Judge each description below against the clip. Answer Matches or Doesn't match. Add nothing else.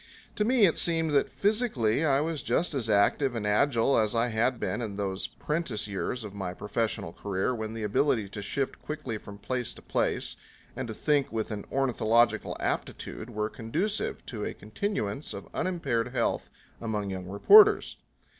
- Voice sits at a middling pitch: Doesn't match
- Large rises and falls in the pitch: Matches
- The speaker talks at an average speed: Matches